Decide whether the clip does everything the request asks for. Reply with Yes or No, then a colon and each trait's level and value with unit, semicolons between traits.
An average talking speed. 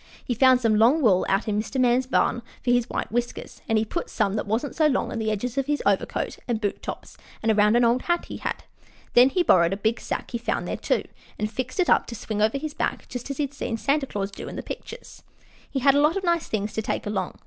No: fast, 270 wpm